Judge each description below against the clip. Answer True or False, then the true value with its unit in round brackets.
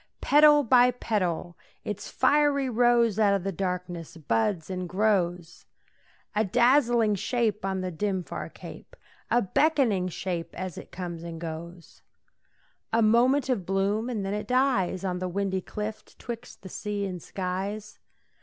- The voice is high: True (200 Hz)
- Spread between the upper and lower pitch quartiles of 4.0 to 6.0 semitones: True (4.6 semitones)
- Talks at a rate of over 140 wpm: True (150 wpm)